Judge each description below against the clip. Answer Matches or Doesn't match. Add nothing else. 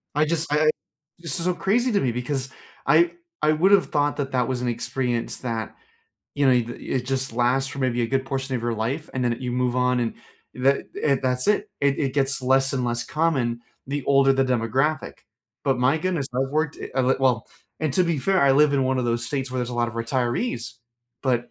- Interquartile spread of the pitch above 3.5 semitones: Doesn't match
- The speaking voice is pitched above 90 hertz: Matches